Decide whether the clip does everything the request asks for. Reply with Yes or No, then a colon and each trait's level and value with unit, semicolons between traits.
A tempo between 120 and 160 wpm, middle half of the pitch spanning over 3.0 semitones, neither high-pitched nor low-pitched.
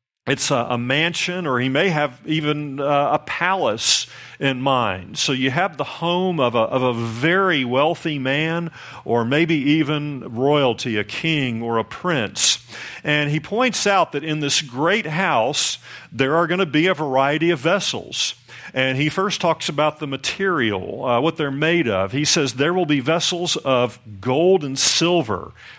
No: average, 175 wpm; average, 4.0 semitones; medium, 145 Hz